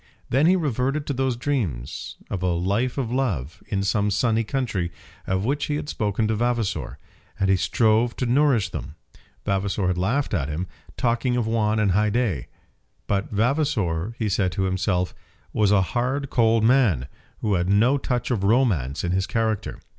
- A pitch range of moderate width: Yes, average, 4.6 semitones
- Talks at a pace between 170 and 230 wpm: Yes, average, 175 wpm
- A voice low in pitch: Yes, low, 110 Hz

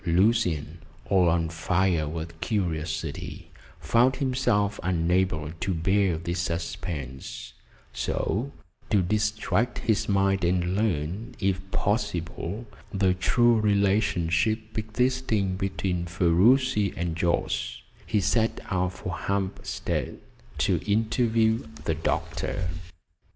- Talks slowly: Yes, slow, 100 wpm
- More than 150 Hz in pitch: No, very low, 95 Hz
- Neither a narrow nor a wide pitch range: Yes, average, 4.0 semitones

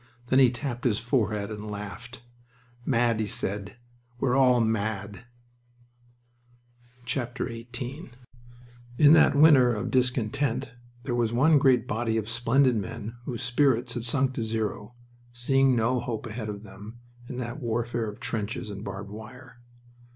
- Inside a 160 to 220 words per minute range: No, average, 140 wpm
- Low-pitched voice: Yes, low, 120 Hz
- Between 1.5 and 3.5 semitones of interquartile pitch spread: Yes, average, 2.7 semitones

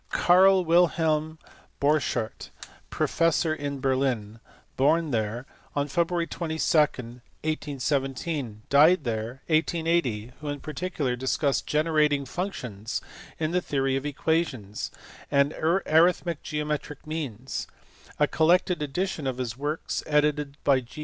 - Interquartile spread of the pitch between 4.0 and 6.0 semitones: No, average, 3.6 semitones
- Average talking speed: No, slow, 115 wpm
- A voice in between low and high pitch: Yes, medium, 150 Hz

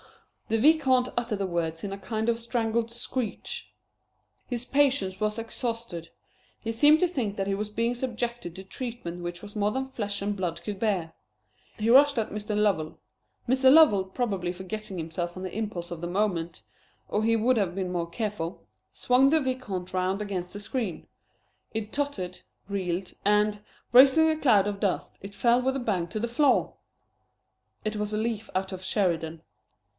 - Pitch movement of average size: Yes, average, 4.3 semitones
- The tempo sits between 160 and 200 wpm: Yes, average, 180 wpm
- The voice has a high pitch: Yes, high, 210 Hz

